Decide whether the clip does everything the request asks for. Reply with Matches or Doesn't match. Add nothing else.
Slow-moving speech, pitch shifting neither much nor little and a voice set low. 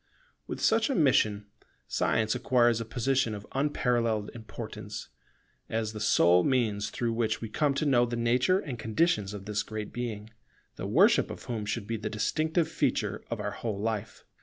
Doesn't match